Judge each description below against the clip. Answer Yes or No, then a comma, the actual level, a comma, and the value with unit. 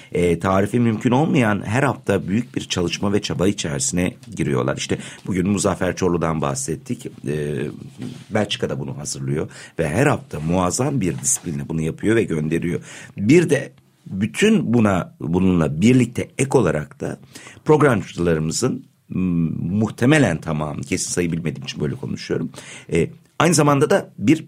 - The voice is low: Yes, very low, 95 Hz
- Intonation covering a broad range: Yes, wide, 7.3 semitones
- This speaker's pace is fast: No, average, 125 wpm